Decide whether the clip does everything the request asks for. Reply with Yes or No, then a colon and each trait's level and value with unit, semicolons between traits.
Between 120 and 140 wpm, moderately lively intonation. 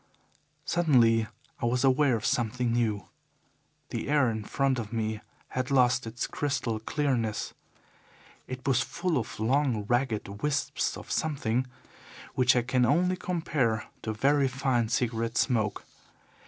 Yes: slow, 135 wpm; average, 3.5 semitones